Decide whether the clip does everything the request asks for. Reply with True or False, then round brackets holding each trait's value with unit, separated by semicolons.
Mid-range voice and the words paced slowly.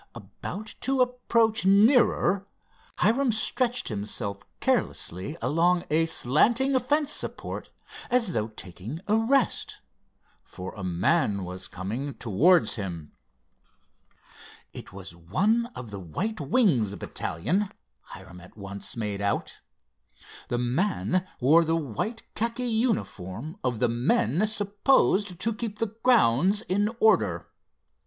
True (165 Hz; 120 wpm)